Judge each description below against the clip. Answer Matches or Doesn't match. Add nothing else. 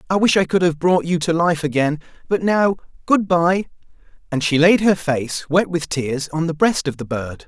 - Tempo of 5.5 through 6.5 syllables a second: Doesn't match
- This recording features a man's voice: Matches